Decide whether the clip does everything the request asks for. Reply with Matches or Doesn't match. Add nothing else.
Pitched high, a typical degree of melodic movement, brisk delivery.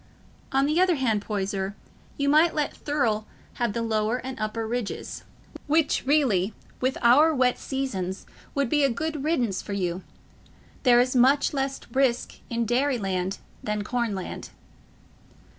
Doesn't match